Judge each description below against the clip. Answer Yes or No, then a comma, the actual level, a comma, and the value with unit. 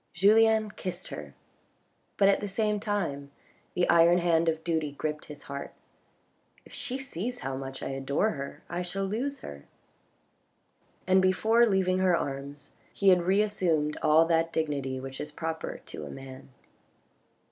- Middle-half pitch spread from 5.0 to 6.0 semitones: Yes, wide, 5.4 semitones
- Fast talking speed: No, average, 155 wpm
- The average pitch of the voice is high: No, medium, 170 Hz